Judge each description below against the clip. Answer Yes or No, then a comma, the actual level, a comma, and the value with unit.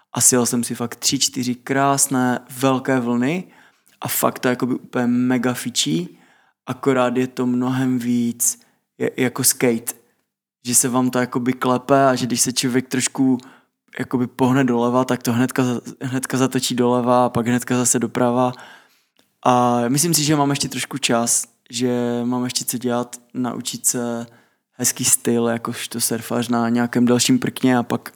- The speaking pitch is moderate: No, low, 125 Hz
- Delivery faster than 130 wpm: Yes, fast, 170 wpm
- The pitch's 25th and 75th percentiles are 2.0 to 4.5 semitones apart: No, narrow, 1.2 semitones